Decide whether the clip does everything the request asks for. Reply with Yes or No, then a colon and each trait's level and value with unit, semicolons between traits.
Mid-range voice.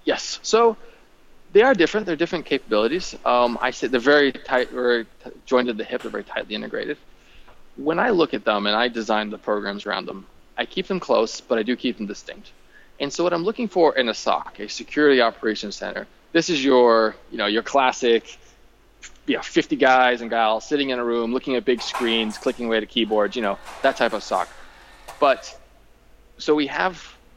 No: low, 125 Hz